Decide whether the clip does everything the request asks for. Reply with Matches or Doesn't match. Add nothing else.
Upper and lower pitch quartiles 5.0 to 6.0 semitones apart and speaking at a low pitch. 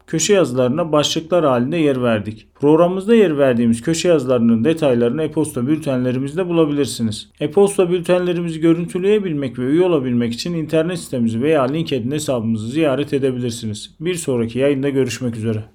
Doesn't match